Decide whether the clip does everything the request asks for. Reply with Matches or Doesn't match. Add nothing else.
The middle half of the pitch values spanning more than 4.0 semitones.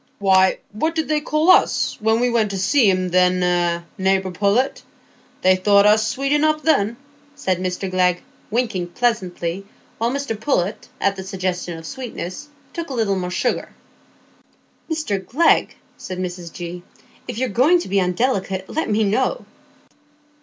Matches